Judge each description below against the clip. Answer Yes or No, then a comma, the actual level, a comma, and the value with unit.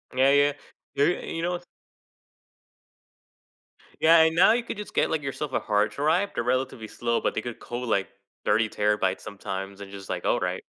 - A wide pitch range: Yes, wide, 7.3 semitones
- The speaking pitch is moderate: No, low, 125 Hz